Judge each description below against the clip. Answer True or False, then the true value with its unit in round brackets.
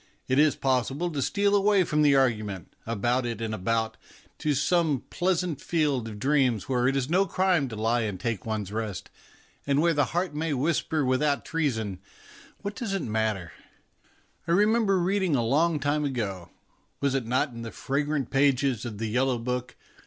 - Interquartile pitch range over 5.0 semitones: True (5.5 semitones)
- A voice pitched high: False (135 Hz)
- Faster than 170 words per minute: True (180 wpm)